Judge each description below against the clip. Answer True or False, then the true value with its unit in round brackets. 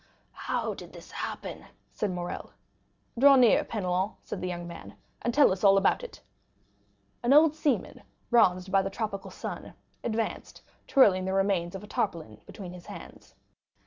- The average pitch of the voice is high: True (195 Hz)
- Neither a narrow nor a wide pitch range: True (4.4 semitones)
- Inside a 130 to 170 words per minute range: True (160 wpm)